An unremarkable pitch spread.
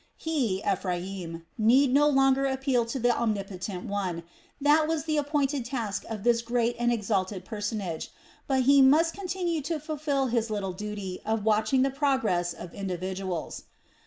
No: wide, 5.9 semitones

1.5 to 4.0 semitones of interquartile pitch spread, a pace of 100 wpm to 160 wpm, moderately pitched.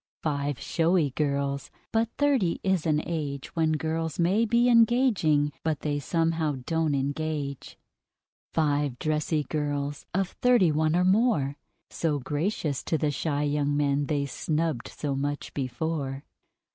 Yes: narrow, 2.6 semitones; slow, 135 wpm; medium, 155 Hz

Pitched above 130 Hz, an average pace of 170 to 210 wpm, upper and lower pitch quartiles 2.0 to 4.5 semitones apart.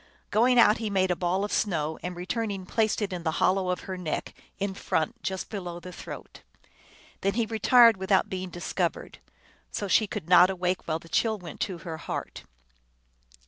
Yes: medium, 185 Hz; average, 195 wpm; average, 2.8 semitones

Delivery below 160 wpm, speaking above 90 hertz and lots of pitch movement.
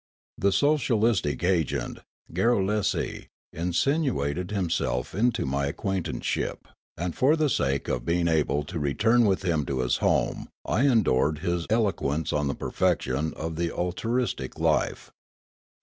No: slow, 135 wpm; very low, 85 Hz; wide, 7.0 semitones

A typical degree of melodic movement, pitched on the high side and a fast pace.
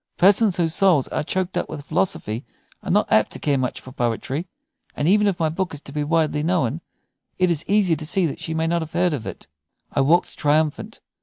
No: average, 3.6 semitones; medium, 160 Hz; fast, 225 wpm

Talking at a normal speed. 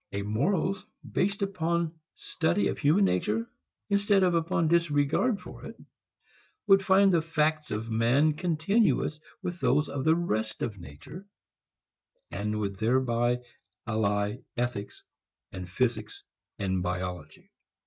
No: slow, 125 wpm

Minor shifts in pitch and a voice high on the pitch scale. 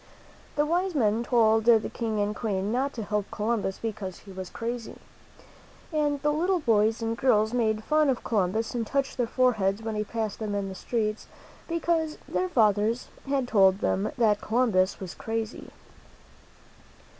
No: average, 3.3 semitones; high, 225 Hz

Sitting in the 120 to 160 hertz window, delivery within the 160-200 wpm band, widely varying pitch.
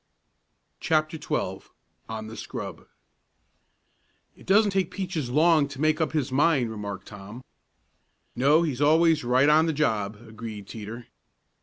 No: medium, 140 Hz; slow, 135 wpm; wide, 6.1 semitones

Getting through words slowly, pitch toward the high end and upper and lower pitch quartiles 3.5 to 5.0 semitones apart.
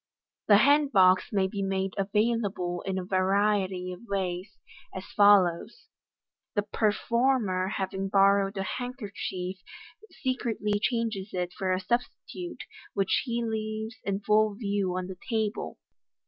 No: slow, 130 wpm; high, 200 Hz; narrow, 2.6 semitones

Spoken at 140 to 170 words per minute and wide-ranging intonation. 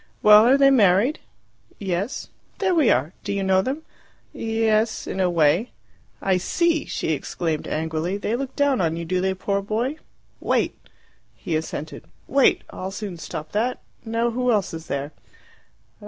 Yes: average, 160 wpm; wide, 5.8 semitones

